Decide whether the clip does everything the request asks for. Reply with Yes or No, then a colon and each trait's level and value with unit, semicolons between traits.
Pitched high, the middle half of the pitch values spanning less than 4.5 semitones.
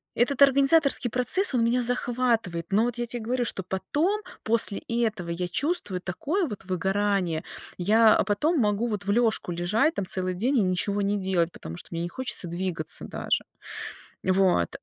No: high, 210 Hz; average, 5.1 semitones